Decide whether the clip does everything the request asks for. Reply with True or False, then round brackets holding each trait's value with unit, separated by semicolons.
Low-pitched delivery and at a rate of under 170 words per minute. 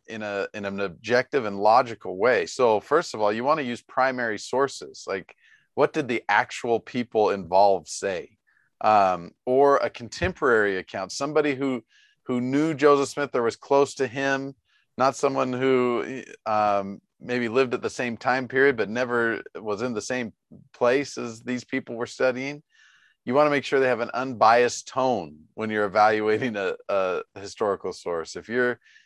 False (125 Hz; 175 wpm)